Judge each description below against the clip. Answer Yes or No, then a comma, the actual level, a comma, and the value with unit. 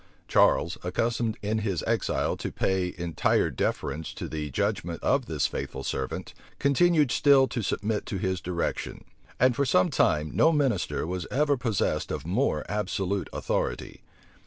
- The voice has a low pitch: Yes, low, 100 Hz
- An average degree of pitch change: No, wide, 6.8 semitones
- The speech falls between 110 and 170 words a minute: Yes, average, 150 wpm